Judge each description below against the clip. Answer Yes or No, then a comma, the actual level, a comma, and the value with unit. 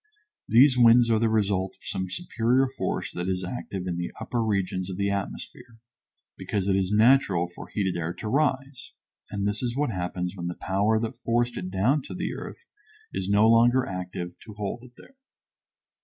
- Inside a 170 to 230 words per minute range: Yes, average, 190 wpm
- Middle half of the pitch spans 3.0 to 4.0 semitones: No, average, 4.5 semitones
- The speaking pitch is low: Yes, low, 105 Hz